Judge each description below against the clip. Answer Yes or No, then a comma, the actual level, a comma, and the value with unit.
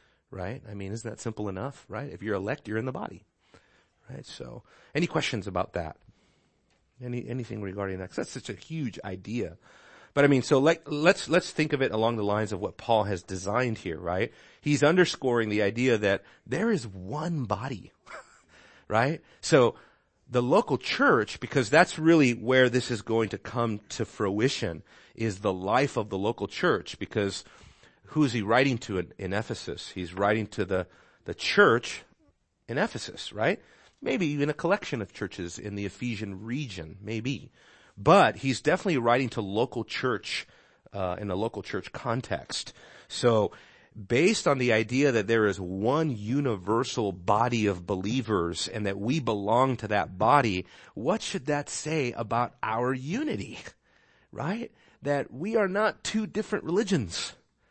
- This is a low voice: Yes, low, 115 Hz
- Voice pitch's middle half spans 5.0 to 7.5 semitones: Yes, wide, 5.6 semitones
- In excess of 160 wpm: Yes, average, 170 wpm